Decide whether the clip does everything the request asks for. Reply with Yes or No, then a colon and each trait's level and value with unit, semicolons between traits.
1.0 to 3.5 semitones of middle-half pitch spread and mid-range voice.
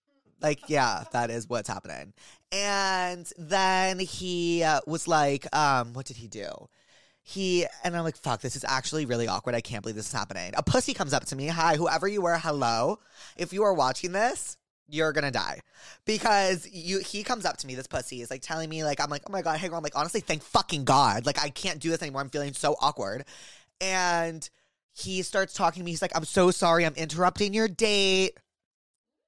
No: average, 5.1 semitones; medium, 165 Hz